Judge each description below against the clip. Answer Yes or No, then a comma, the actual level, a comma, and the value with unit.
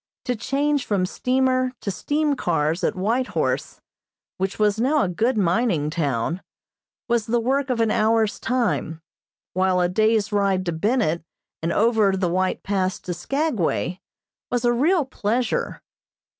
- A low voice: No, high, 215 Hz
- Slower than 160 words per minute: Yes, average, 150 wpm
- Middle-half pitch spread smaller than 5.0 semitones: No, wide, 5.4 semitones